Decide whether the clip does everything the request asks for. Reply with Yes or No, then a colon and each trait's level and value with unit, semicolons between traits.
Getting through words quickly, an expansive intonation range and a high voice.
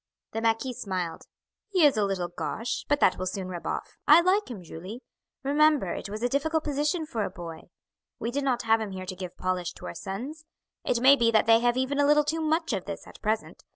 Yes: fast, 235 wpm; wide, 7.2 semitones; high, 230 Hz